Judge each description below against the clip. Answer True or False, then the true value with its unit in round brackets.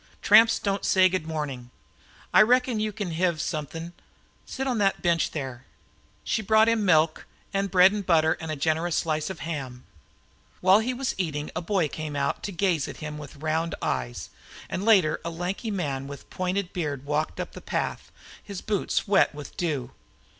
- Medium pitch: True (170 Hz)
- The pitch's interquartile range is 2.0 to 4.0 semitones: False (4.6 semitones)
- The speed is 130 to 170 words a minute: False (180 wpm)